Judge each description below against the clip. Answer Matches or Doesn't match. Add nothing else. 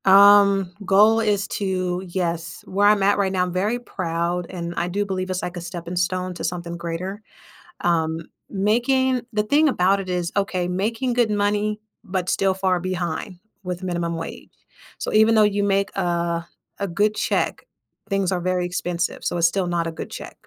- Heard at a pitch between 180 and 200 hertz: Matches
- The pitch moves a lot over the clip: Doesn't match